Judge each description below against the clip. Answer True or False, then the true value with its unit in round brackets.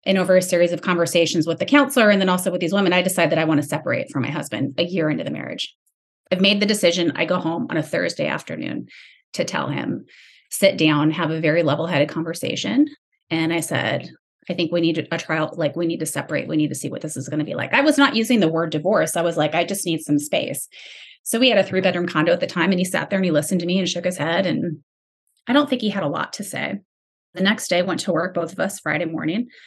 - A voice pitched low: False (170 Hz)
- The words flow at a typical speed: False (270 wpm)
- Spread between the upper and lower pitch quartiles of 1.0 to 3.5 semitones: True (3.2 semitones)